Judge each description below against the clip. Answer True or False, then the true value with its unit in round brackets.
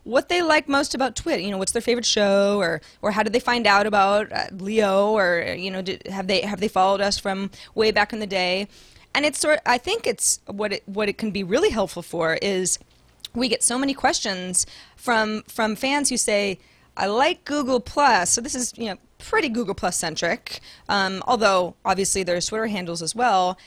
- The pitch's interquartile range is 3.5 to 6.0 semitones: True (4.2 semitones)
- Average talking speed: False (215 wpm)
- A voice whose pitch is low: False (210 Hz)